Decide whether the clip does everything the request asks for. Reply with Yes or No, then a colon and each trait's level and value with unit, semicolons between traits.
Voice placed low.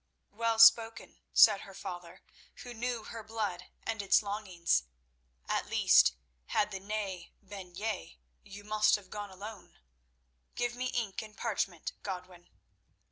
No: high, 205 Hz